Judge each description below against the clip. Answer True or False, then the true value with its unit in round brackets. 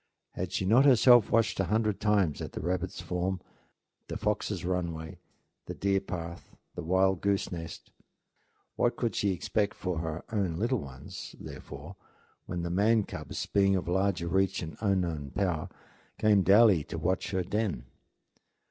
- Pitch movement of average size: True (3.0 semitones)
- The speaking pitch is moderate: False (95 Hz)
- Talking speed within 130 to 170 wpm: True (160 wpm)